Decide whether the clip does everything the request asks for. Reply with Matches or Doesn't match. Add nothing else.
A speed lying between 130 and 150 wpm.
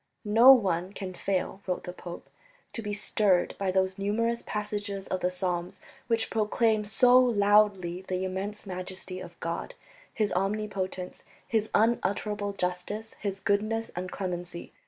Matches